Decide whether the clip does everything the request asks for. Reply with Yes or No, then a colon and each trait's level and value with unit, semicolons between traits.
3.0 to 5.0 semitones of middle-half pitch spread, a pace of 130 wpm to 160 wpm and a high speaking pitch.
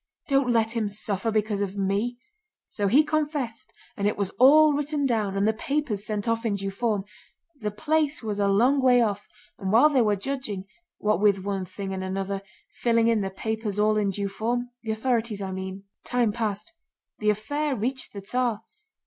No: average, 3.6 semitones; average, 185 wpm; high, 215 Hz